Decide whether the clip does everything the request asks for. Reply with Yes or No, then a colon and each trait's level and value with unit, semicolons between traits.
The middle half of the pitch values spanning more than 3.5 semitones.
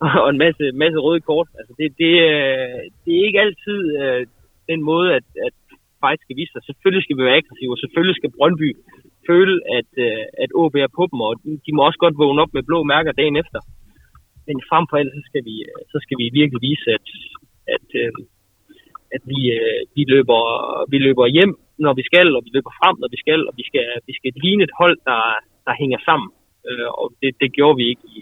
Yes: average, 4.1 semitones